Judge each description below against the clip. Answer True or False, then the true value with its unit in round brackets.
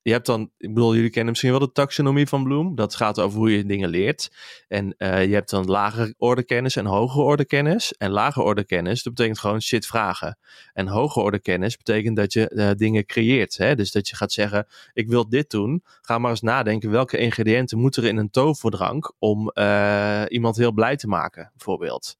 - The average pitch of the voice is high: False (115 Hz)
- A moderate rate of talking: False (215 wpm)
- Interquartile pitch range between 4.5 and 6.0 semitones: False (2.8 semitones)